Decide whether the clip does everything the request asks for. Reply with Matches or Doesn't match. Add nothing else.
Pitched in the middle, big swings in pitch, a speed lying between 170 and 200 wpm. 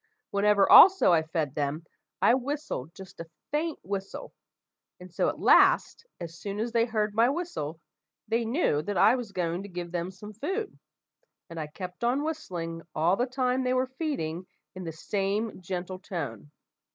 Doesn't match